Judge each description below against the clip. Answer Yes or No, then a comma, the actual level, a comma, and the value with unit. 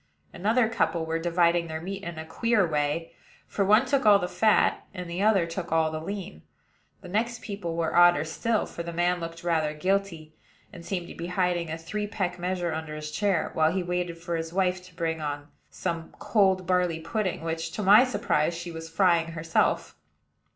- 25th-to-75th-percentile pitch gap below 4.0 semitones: Yes, average, 3.0 semitones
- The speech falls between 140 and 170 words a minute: No, average, 195 wpm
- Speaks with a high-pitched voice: No, medium, 175 Hz